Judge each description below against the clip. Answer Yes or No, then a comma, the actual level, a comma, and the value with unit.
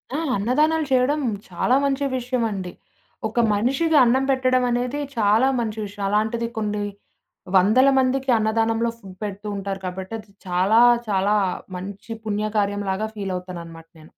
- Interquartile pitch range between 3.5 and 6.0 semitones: Yes, average, 4.2 semitones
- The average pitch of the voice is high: Yes, high, 215 Hz